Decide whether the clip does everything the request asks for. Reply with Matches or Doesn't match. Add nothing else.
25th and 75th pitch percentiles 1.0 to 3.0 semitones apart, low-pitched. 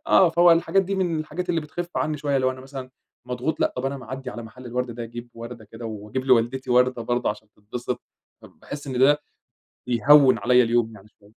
Doesn't match